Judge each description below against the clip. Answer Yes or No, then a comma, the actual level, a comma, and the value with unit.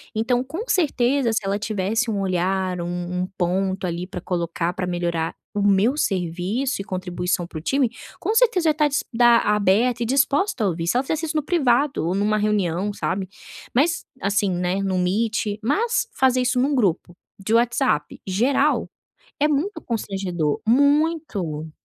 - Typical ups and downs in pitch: No, wide, 6.7 semitones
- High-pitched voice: Yes, high, 210 Hz